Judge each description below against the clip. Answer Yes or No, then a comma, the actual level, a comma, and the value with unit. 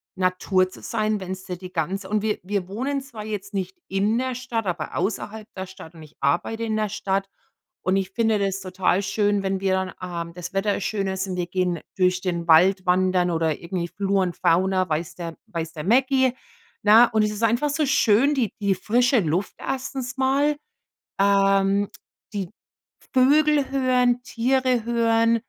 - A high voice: Yes, high, 200 Hz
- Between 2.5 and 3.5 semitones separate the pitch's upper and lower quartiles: No, average, 3.9 semitones